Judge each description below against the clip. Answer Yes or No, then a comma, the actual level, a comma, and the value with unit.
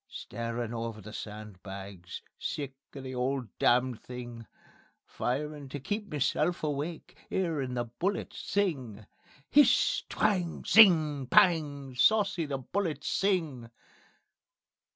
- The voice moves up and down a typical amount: No, wide, 5.8 semitones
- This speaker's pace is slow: Yes, slow, 110 wpm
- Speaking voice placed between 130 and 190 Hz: Yes, low, 135 Hz